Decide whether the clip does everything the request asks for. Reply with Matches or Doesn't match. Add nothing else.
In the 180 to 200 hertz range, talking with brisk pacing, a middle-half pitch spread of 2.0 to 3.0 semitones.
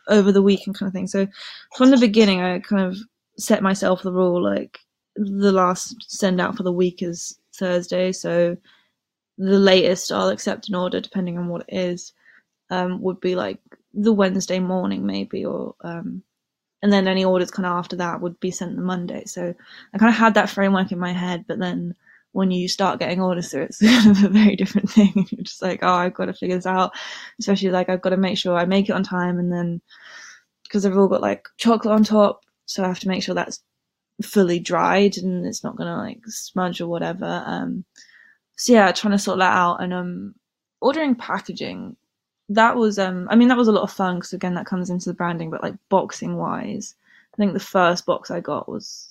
Matches